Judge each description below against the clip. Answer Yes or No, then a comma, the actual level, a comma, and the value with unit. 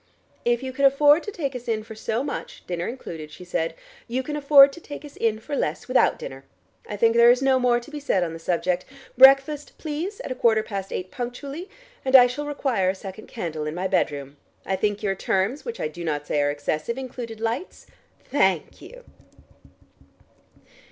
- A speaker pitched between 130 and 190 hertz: No, high, 235 Hz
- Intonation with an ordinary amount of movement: No, wide, 6.8 semitones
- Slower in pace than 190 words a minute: No, fast, 205 wpm